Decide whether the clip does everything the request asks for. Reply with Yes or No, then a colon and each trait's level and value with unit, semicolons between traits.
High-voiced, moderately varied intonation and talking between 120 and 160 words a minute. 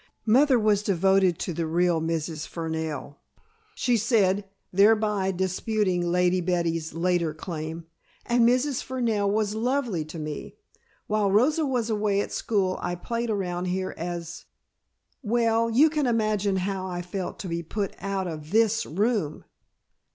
Yes: high, 195 Hz; average, 4.4 semitones; average, 145 wpm